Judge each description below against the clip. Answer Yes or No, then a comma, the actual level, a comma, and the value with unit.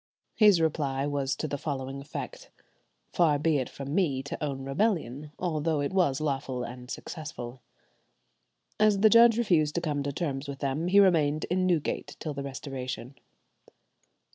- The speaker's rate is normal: Yes, average, 160 wpm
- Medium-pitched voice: Yes, medium, 145 Hz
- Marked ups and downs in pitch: No, average, 4.1 semitones